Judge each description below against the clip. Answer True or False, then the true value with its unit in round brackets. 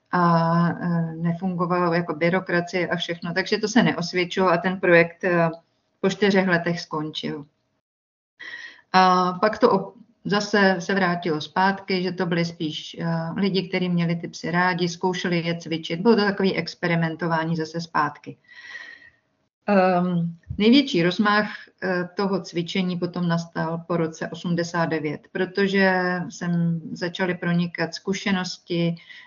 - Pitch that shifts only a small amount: True (2.3 semitones)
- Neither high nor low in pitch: True (180 Hz)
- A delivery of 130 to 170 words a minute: False (120 wpm)